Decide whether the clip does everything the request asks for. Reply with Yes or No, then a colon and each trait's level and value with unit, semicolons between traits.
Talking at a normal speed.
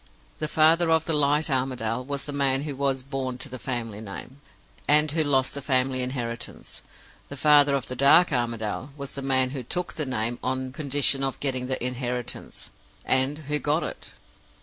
Yes: average, 185 wpm